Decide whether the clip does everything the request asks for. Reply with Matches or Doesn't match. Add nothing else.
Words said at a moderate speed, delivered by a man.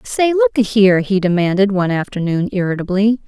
Doesn't match